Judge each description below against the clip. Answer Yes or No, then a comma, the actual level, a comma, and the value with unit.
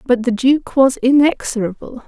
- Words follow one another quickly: No, average, 145 wpm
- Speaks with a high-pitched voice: Yes, very high, 255 Hz